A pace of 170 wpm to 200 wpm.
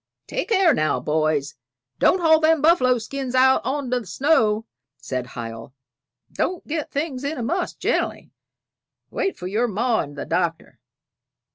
No: average, 155 wpm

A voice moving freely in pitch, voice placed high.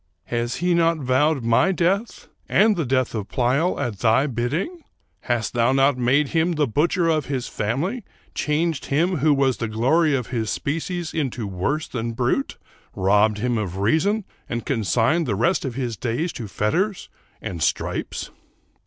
No: wide, 6.0 semitones; low, 135 Hz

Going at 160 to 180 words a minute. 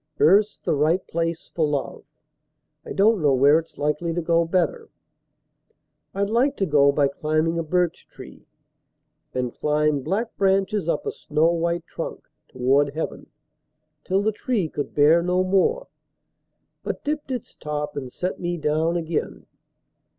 No: average, 150 wpm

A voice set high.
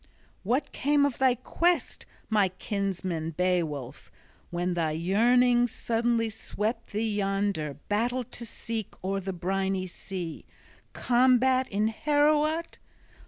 Yes: high, 215 Hz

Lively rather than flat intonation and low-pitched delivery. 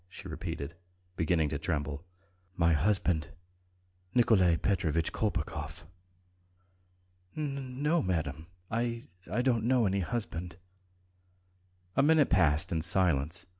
Yes: wide, 6.8 semitones; very low, 90 Hz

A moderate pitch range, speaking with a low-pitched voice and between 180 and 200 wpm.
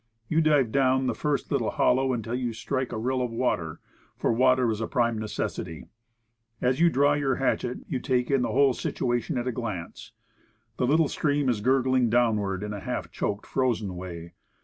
Yes: average, 3.0 semitones; low, 125 Hz; average, 195 wpm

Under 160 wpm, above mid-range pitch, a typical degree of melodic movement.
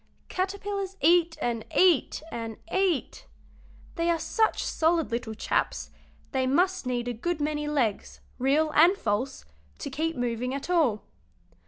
No: average, 140 wpm; very high, 300 Hz; wide, 6.1 semitones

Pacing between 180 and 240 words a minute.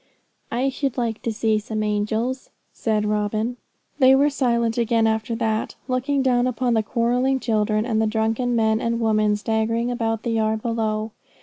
No: average, 170 wpm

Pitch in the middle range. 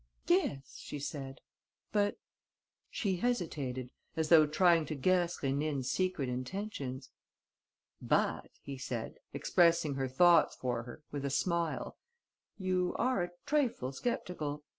Yes: medium, 155 Hz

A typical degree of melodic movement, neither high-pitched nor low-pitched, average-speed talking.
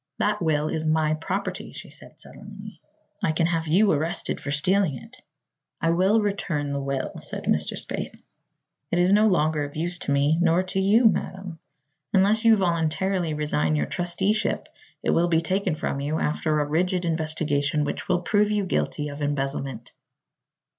Yes: average, 4.1 semitones; medium, 165 Hz; average, 170 wpm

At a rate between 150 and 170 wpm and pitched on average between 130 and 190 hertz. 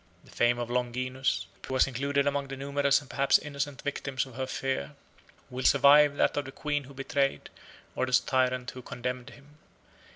No: average, 185 wpm; low, 135 Hz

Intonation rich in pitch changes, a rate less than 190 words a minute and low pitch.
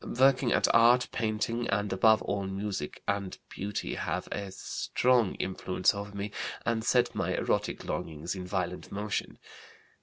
No: average, 3.4 semitones; average, 145 wpm; low, 105 Hz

